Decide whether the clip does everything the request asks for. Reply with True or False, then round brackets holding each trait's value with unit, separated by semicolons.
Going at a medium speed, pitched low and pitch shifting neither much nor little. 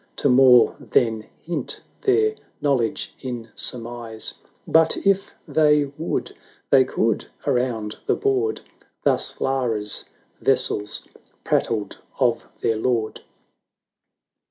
False (110 wpm; 125 Hz; 4.9 semitones)